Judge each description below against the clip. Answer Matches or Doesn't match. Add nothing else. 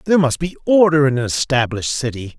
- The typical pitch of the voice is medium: Matches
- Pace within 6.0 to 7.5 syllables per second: Matches